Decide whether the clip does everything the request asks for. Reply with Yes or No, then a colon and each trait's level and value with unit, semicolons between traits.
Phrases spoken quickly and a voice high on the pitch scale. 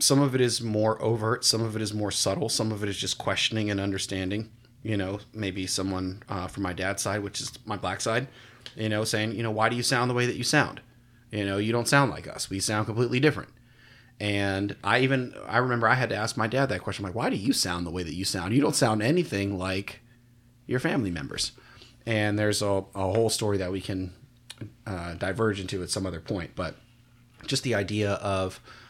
No: fast, 235 wpm; low, 110 Hz